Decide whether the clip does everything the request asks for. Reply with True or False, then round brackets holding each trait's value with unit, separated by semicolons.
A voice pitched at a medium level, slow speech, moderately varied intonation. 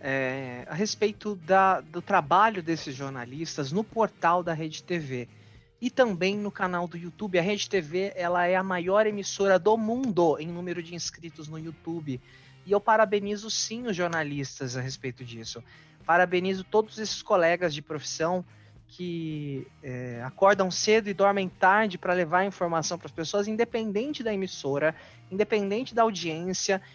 False (175 Hz; 155 wpm; 4.9 semitones)